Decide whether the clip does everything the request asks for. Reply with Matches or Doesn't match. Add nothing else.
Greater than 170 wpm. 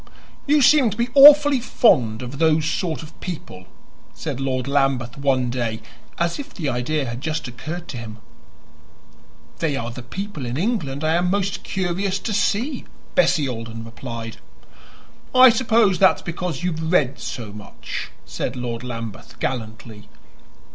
Doesn't match